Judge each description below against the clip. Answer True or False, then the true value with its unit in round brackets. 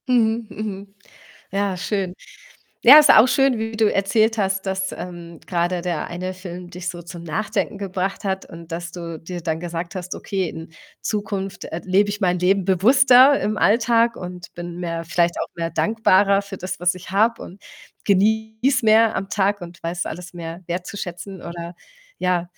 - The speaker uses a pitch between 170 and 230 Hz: True (190 Hz)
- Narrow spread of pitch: False (3.4 semitones)